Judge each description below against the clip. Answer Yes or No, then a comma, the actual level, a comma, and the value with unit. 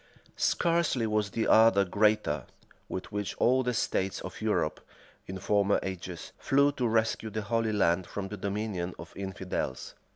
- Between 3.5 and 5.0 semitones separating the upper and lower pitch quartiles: No, average, 2.8 semitones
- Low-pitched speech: Yes, low, 105 Hz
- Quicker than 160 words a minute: No, average, 155 wpm